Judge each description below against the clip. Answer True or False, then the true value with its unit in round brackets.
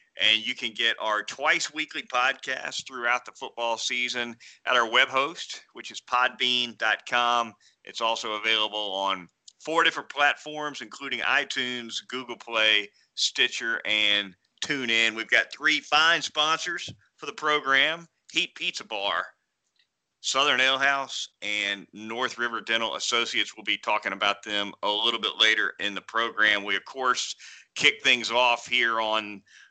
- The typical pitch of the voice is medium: False (120 Hz)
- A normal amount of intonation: True (3.6 semitones)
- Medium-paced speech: True (145 wpm)